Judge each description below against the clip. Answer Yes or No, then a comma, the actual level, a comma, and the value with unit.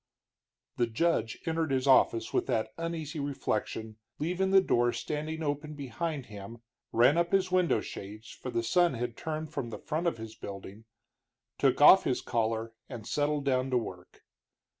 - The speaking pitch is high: No, low, 135 Hz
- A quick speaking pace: No, average, 165 wpm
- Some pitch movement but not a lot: No, wide, 5.9 semitones